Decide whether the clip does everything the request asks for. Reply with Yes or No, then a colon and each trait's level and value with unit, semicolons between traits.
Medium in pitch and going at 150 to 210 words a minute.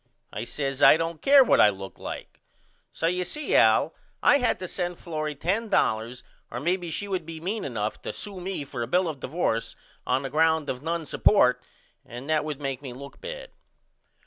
Yes: medium, 160 Hz; average, 200 wpm